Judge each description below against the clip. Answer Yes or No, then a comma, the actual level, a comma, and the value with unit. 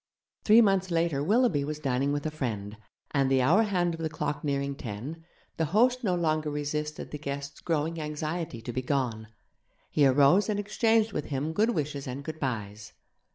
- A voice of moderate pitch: Yes, medium, 150 Hz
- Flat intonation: No, average, 3.8 semitones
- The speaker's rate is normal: Yes, average, 180 wpm